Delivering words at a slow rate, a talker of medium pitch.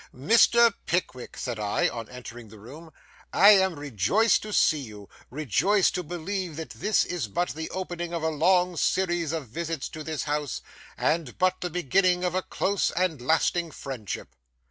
No: average, 165 wpm; medium, 165 Hz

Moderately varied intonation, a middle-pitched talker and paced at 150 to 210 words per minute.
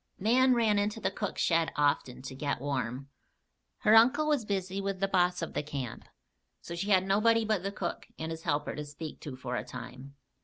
No: wide, 6.3 semitones; medium, 180 Hz; fast, 205 wpm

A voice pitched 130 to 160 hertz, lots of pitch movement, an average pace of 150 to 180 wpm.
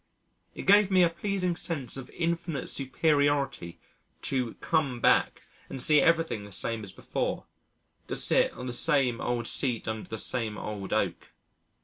Yes: low, 135 Hz; wide, 6.0 semitones; average, 155 wpm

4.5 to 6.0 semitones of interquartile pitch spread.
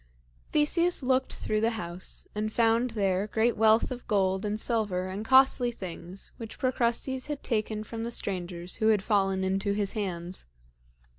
No: average, 3.6 semitones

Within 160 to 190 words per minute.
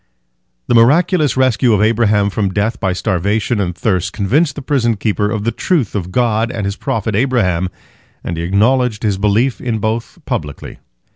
Yes: average, 170 wpm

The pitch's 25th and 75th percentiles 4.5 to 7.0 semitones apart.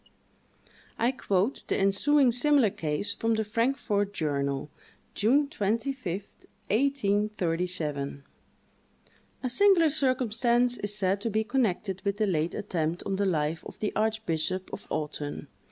Yes: wide, 5.5 semitones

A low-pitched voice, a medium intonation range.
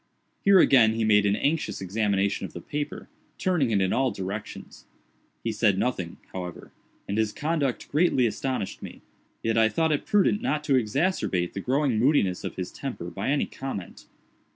No: low, 115 Hz; wide, 6.4 semitones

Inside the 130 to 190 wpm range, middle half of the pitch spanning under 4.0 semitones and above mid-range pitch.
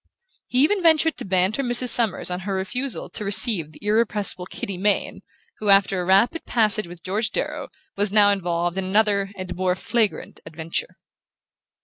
Yes: average, 165 wpm; average, 3.4 semitones; high, 200 Hz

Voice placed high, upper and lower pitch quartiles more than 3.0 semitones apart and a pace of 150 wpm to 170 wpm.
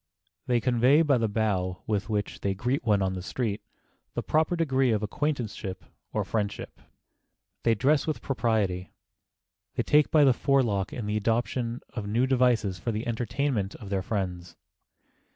No: low, 115 Hz; average, 4.3 semitones; average, 165 wpm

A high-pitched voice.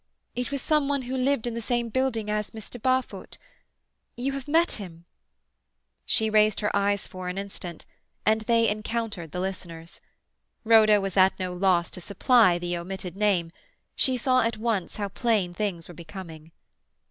Yes: high, 210 Hz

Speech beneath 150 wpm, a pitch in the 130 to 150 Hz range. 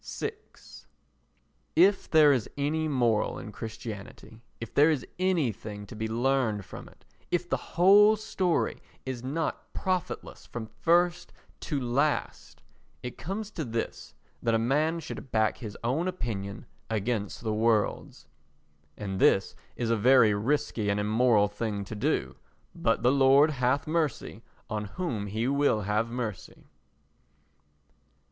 No: slow, 135 wpm; low, 120 Hz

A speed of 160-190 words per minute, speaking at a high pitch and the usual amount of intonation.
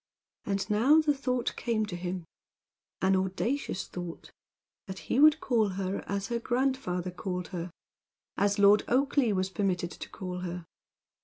No: average, 150 wpm; high, 200 Hz; average, 4.9 semitones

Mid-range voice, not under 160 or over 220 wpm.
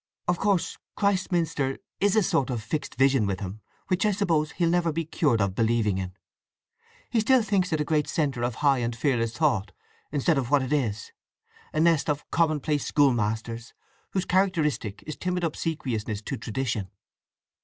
Yes: medium, 145 Hz; average, 170 wpm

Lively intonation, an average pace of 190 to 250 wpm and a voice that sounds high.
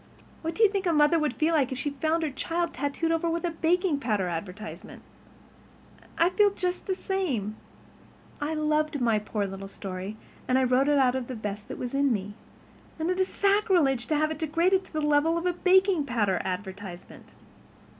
Yes: wide, 6.5 semitones; average, 200 wpm; very high, 295 Hz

